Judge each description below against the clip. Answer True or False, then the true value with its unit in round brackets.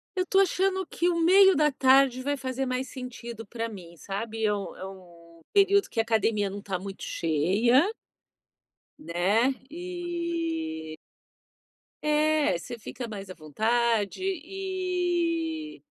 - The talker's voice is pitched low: False (255 Hz)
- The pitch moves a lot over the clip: True (9.0 semitones)